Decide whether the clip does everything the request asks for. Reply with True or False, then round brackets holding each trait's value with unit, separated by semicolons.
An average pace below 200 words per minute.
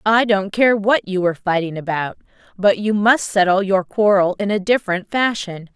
True (190 wpm)